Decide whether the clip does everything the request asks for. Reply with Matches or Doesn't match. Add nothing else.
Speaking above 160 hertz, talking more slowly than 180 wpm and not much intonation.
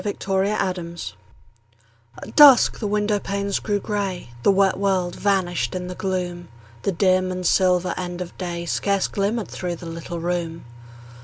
Matches